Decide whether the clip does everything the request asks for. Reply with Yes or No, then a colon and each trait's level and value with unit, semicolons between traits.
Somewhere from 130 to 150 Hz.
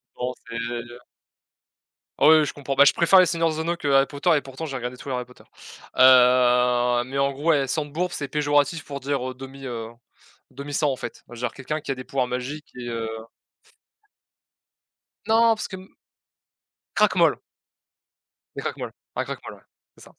Yes: low, 135 Hz